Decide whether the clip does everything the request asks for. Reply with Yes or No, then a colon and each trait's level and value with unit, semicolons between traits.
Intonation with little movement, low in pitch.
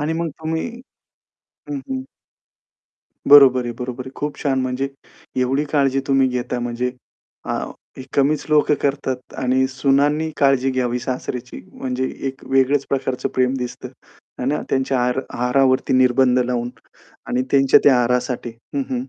Yes: narrow, 1.9 semitones; low, 130 Hz